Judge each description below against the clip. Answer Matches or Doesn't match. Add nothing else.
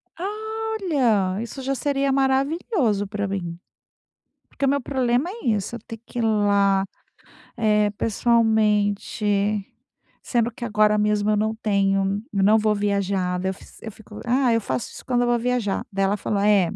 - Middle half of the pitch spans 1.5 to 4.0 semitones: Matches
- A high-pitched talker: Matches